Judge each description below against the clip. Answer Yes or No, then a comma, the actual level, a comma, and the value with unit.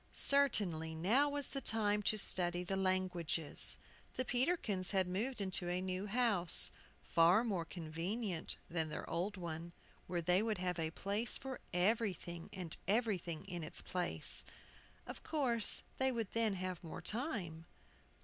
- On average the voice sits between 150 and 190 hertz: Yes, medium, 185 Hz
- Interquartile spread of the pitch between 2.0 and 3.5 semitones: No, average, 4.5 semitones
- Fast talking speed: No, average, 150 wpm